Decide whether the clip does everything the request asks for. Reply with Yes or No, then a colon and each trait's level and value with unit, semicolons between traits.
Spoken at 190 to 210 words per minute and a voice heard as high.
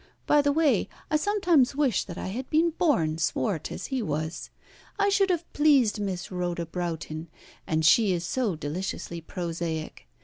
No: average, 165 wpm; high, 195 Hz